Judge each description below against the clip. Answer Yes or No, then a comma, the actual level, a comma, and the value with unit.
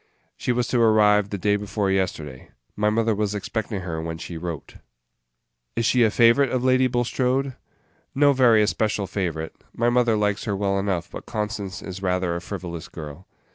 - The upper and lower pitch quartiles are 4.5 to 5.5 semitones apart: No, average, 4.1 semitones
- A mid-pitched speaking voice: No, low, 105 Hz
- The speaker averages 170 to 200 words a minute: Yes, average, 175 wpm